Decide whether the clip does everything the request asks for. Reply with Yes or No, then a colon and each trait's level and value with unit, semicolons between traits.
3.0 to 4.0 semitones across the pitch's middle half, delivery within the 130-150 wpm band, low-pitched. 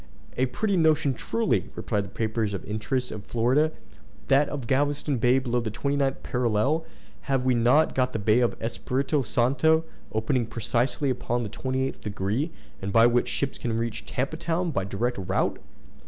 No: average, 3.6 semitones; average, 170 wpm; low, 125 Hz